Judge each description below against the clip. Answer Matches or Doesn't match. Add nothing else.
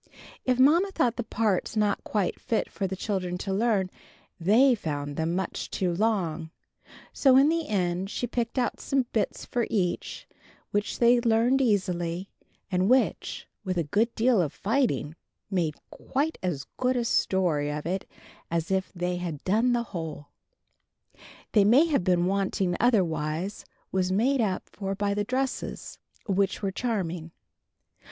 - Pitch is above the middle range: Matches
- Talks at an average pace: Matches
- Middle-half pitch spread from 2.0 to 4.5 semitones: Doesn't match